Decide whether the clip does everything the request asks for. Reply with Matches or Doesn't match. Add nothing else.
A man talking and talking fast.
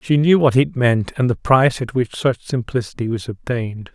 Matches